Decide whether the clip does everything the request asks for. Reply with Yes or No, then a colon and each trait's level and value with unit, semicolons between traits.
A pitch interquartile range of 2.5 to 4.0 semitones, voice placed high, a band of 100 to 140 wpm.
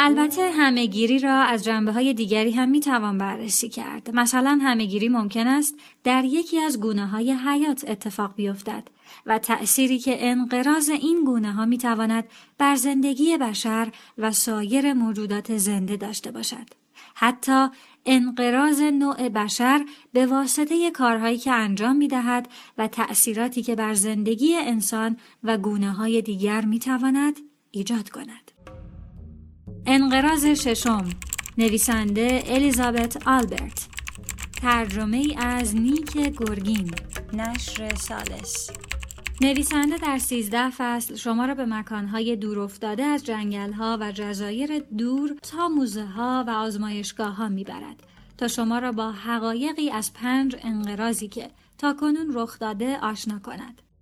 Yes: average, 3.6 semitones; high, 235 Hz; average, 125 wpm